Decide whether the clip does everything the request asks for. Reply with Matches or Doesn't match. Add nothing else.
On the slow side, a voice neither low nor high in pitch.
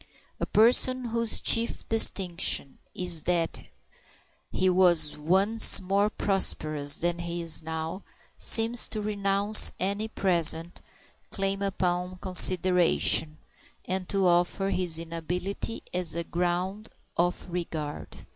Matches